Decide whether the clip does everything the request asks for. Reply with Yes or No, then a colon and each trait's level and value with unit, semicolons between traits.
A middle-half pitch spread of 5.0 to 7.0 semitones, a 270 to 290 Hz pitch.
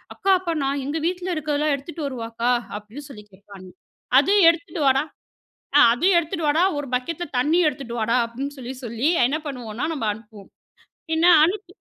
Yes: wide, 5.5 semitones; very high, 280 Hz